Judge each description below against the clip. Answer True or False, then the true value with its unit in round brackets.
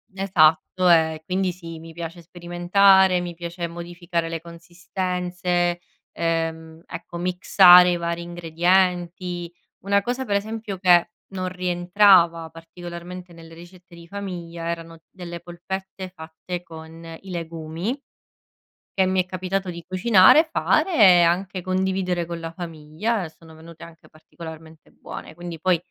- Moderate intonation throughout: False (1.8 semitones)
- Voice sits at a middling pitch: True (175 Hz)